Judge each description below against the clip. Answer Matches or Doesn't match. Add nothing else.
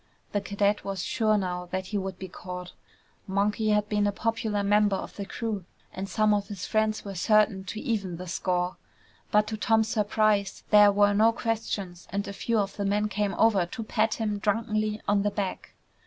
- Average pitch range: Doesn't match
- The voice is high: Matches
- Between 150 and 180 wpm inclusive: Doesn't match